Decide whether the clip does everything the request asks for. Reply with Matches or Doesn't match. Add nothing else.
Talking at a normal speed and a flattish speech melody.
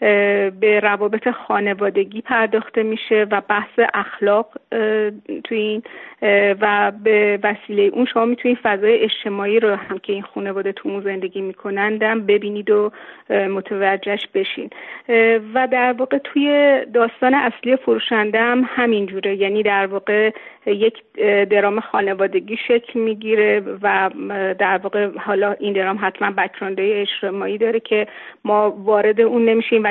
Matches